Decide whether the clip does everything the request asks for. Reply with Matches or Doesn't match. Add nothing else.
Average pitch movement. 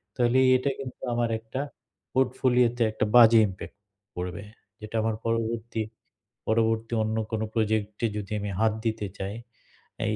Doesn't match